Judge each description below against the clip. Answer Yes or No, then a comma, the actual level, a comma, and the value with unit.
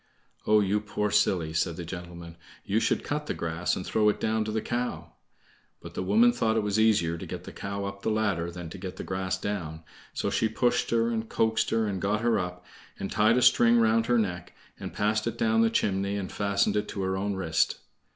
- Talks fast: Yes, fast, 230 wpm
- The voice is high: No, low, 100 Hz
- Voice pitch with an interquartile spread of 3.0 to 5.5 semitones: Yes, average, 3.3 semitones